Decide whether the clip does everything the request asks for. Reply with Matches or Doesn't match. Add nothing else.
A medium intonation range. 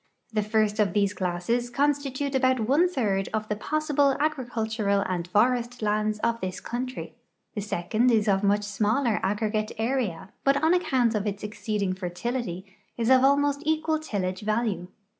Matches